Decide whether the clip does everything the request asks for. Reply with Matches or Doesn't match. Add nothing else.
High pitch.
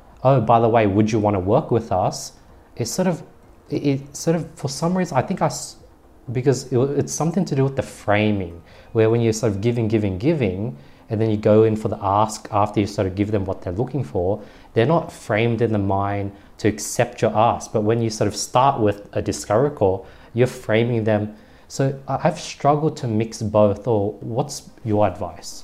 Doesn't match